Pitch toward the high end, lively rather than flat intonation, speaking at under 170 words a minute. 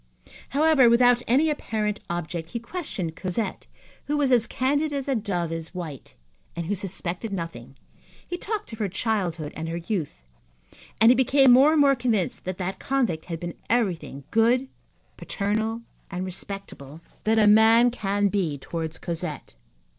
Yes: high, 205 Hz; wide, 6.1 semitones; average, 160 wpm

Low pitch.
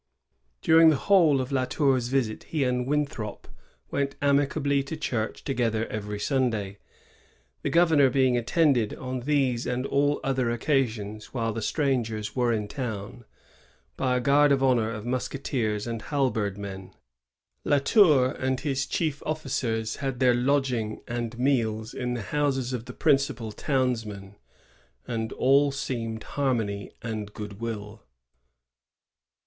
Yes: low, 125 Hz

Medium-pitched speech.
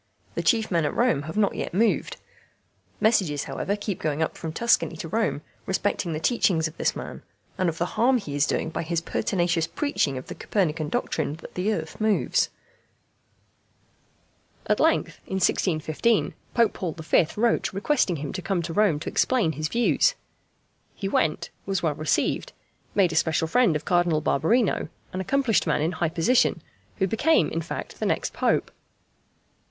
Yes: medium, 175 Hz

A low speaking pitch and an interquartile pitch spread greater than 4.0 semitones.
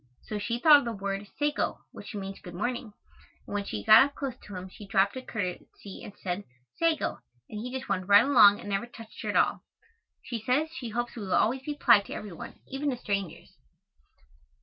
No: high, 215 Hz; average, 4.4 semitones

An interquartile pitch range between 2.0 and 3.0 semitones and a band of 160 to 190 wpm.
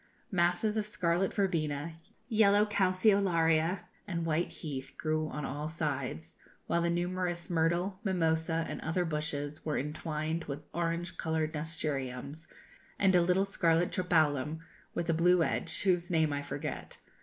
No: narrow, 2.5 semitones; average, 140 wpm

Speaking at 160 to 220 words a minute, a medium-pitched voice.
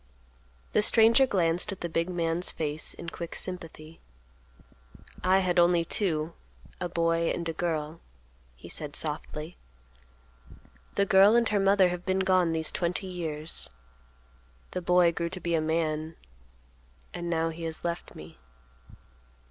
No: average, 145 wpm; medium, 170 Hz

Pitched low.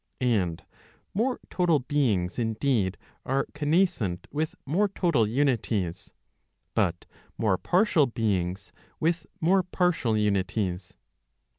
Yes: low, 125 Hz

